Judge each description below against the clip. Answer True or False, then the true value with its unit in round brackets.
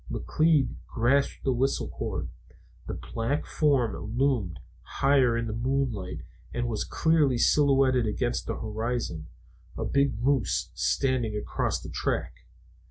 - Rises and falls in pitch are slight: False (3.3 semitones)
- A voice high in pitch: False (125 Hz)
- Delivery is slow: True (125 wpm)